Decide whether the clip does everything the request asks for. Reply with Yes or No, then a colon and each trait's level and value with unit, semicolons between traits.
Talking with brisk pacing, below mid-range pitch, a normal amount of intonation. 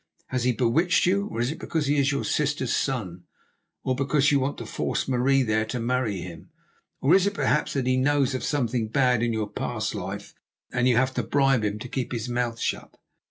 Yes: fast, 220 wpm; low, 130 Hz; average, 3.1 semitones